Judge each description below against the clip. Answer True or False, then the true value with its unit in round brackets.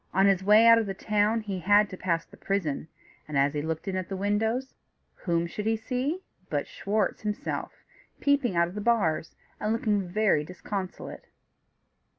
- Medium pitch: False (205 Hz)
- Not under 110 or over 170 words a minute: False (180 wpm)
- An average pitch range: True (3.6 semitones)